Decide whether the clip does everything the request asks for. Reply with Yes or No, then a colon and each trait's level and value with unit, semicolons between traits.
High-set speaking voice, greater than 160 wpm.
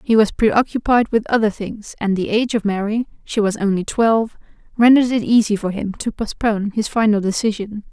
Yes: high, 215 Hz; average, 175 wpm